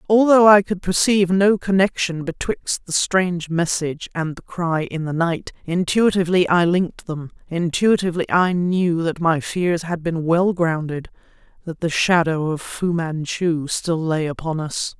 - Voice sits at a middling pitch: Yes, medium, 170 Hz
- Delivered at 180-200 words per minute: No, average, 160 wpm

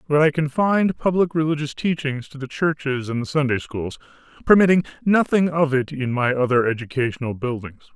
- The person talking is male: Yes, male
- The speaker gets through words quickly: No, average, 165 wpm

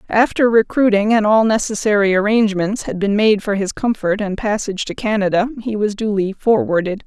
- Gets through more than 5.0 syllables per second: Yes, 5.5 syllables/s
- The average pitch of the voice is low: No, high, 210 Hz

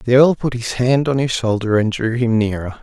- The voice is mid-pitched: No, low, 120 Hz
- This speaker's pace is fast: Yes, fast, 255 wpm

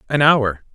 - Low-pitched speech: Yes, low, 125 Hz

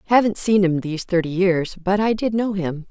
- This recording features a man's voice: No, female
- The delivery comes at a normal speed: No, fast, 225 wpm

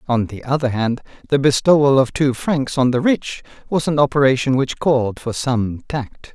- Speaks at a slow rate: No, average, 190 wpm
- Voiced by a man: Yes, male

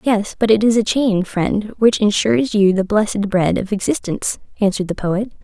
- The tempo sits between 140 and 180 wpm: No, average, 200 wpm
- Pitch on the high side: Yes, high, 205 Hz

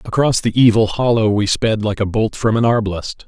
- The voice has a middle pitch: No, low, 110 Hz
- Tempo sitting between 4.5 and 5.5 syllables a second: Yes, 5.1 syllables/s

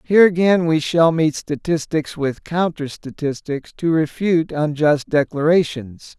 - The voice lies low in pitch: No, medium, 155 Hz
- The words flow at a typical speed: No, slow, 125 wpm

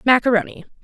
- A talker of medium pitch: No, high, 215 Hz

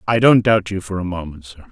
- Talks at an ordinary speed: No, fast, 280 wpm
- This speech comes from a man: Yes, male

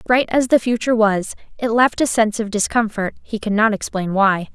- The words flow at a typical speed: No, fast, 210 wpm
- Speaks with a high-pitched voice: Yes, high, 220 Hz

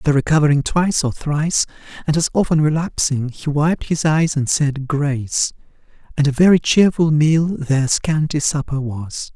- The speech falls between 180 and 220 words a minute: No, average, 160 wpm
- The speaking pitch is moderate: Yes, medium, 150 Hz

